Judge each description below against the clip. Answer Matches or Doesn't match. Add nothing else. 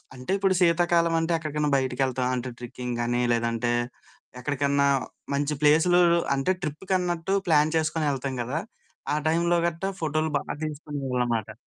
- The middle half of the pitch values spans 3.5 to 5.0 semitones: Matches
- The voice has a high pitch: Doesn't match